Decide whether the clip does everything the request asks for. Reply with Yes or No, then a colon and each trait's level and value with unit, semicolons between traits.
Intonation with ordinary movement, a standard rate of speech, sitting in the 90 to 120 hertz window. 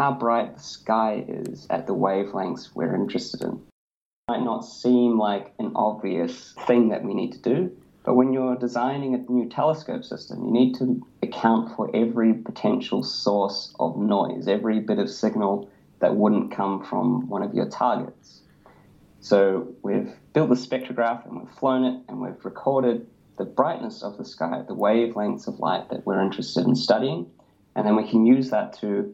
Yes: average, 3.1 semitones; average, 180 wpm; low, 115 Hz